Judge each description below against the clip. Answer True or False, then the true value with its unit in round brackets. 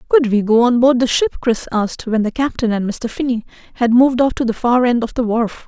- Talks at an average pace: False (265 wpm)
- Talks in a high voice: True (240 Hz)